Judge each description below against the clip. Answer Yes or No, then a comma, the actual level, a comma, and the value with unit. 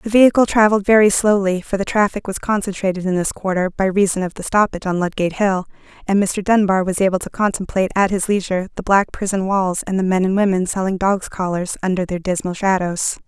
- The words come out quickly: Yes, fast, 210 wpm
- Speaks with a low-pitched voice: No, high, 190 Hz